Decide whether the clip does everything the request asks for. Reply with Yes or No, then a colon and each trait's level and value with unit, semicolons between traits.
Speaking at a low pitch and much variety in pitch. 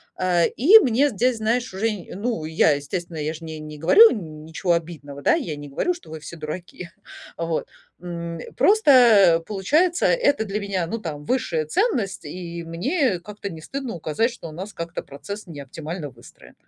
No: medium, 175 Hz; wide, 6.2 semitones